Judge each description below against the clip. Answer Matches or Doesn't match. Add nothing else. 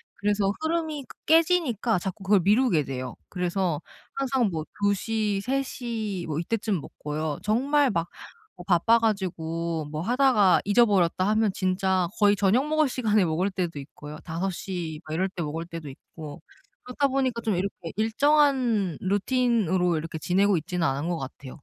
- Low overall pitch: Doesn't match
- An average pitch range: Doesn't match